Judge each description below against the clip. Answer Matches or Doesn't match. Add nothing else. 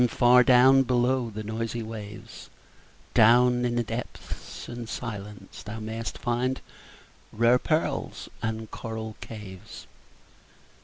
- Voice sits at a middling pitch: Doesn't match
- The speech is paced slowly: Matches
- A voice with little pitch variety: Matches